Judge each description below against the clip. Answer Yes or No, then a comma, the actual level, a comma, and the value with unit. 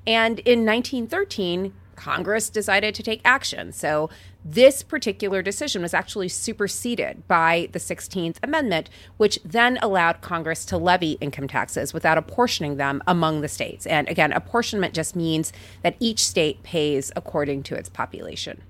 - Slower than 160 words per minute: Yes, average, 150 wpm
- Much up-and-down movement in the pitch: Yes, wide, 5.8 semitones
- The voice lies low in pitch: No, medium, 180 Hz